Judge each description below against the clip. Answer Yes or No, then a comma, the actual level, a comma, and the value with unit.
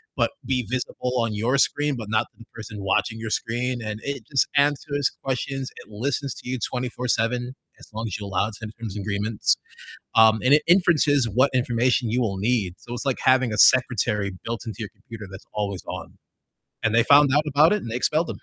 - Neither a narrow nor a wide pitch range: Yes, average, 3.4 semitones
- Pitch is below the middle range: Yes, low, 120 Hz